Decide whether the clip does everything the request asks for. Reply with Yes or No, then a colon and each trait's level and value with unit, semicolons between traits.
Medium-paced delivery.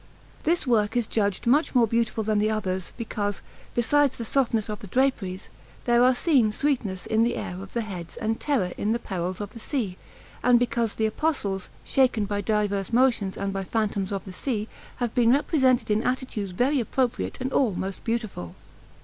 Yes: average, 190 wpm